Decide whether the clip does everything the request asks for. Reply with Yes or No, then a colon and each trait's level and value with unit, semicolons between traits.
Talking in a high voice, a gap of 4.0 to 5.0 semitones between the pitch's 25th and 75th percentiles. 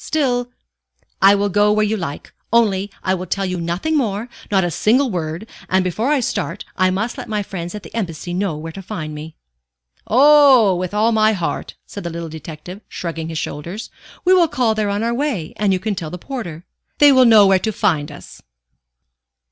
Yes: high, 200 Hz; average, 4.6 semitones